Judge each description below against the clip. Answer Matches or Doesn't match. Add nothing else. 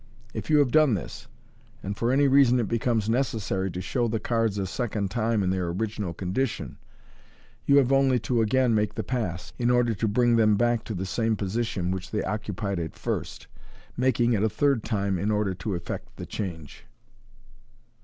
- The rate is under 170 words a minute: Doesn't match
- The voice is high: Doesn't match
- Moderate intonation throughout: Matches